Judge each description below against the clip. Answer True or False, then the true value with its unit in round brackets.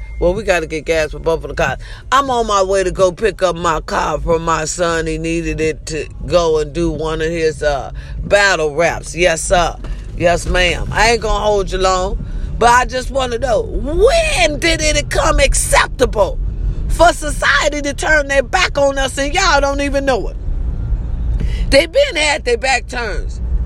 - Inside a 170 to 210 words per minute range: True (200 wpm)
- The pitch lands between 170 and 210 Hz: True (185 Hz)